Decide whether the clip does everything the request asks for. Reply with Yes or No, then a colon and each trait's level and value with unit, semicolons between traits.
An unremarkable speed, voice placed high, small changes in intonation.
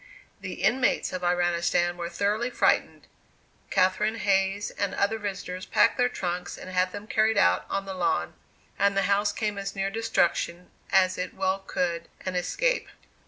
Yes: average, 165 wpm; high, 195 Hz; narrow, 2.2 semitones